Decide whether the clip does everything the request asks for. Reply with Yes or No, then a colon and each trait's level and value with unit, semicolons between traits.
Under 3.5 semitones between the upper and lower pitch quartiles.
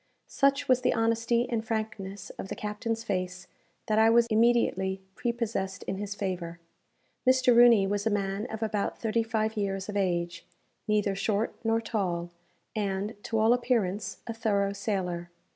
Yes: average, 2.8 semitones